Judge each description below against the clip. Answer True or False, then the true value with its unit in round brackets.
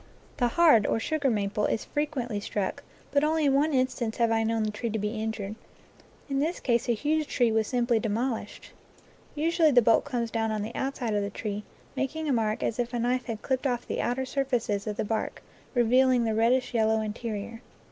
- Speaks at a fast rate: True (210 wpm)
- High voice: True (235 Hz)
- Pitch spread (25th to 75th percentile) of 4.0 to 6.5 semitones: False (3.3 semitones)